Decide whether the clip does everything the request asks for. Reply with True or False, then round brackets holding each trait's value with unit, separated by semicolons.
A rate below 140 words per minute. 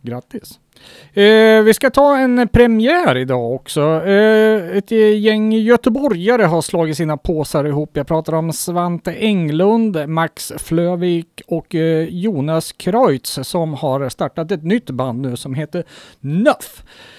True (125 wpm)